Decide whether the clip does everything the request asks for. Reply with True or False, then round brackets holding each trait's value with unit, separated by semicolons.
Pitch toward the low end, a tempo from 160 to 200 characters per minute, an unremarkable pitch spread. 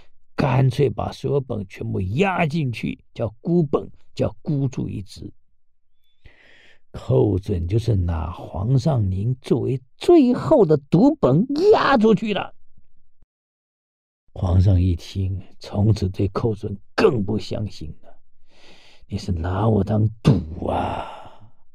False (105 Hz; 165 characters per minute; 6.8 semitones)